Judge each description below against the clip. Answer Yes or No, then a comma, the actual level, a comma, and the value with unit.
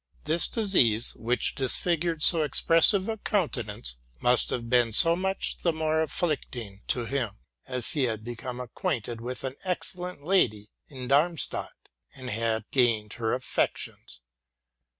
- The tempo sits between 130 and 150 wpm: Yes, average, 140 wpm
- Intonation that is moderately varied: No, wide, 6.2 semitones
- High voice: No, low, 130 Hz